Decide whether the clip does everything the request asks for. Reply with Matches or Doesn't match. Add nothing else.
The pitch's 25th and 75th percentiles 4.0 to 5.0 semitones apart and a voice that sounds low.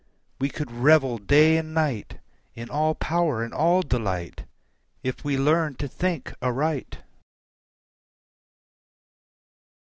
Doesn't match